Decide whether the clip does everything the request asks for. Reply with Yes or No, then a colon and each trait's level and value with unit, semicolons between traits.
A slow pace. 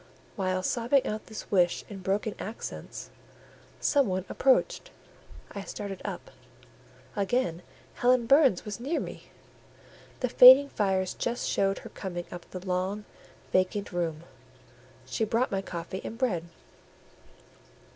Yes: slow, 125 wpm